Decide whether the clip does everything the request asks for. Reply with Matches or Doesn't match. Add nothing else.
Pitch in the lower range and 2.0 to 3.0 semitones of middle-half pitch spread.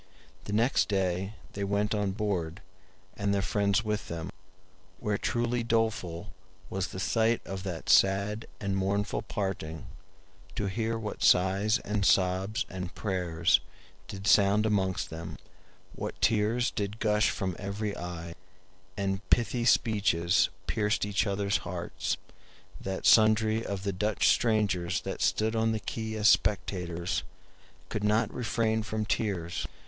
Matches